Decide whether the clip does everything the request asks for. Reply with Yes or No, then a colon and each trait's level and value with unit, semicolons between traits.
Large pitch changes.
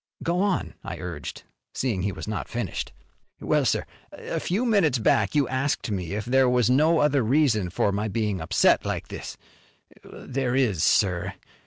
Yes: wide, 5.9 semitones